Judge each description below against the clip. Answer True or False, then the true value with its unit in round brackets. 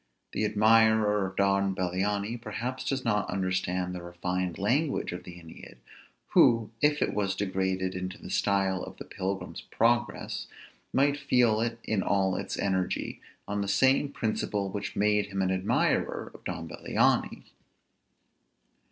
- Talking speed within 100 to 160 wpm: True (145 wpm)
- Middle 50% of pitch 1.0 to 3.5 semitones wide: True (3.0 semitones)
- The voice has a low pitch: True (100 Hz)